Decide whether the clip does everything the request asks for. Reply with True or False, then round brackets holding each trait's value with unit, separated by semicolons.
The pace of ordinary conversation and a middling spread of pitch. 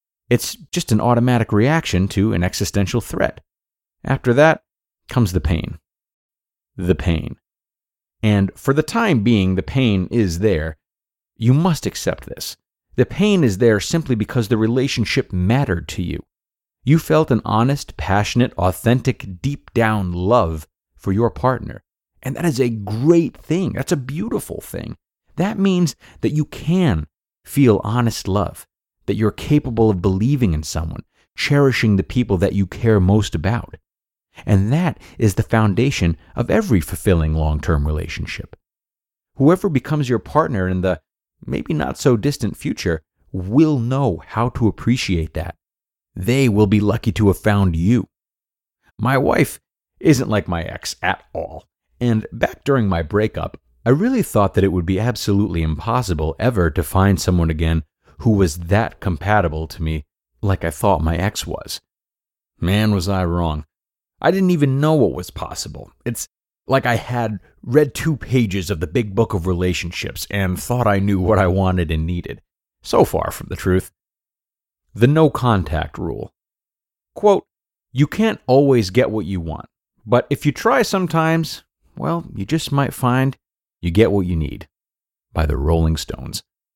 False (160 wpm; 6.0 semitones)